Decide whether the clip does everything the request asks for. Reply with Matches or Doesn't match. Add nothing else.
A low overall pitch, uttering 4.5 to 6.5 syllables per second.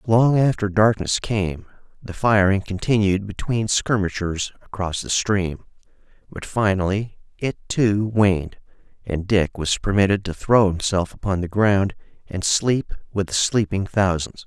Doesn't match